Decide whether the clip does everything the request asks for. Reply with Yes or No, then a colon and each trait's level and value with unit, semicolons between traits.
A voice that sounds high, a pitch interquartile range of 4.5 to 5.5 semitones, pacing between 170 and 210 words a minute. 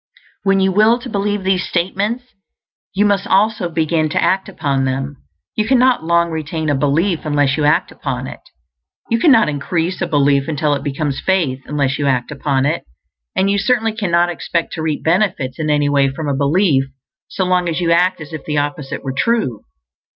No: medium, 160 Hz; average, 5.1 semitones; average, 195 wpm